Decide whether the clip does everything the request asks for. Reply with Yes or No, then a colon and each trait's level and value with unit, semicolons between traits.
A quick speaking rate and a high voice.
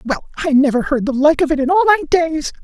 Yes: fast, 275 wpm; very high, 295 Hz